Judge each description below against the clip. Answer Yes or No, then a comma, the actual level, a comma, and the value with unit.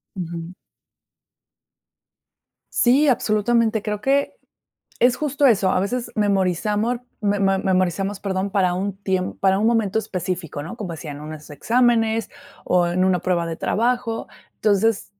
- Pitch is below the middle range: No, high, 200 Hz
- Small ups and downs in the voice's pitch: No, average, 3.7 semitones